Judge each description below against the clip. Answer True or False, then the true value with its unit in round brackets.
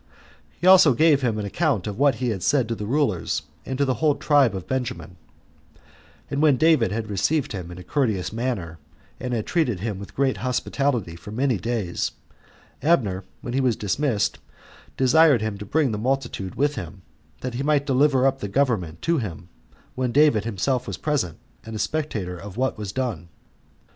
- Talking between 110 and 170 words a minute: False (190 wpm)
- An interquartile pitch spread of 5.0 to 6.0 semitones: True (5.6 semitones)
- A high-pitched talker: False (120 Hz)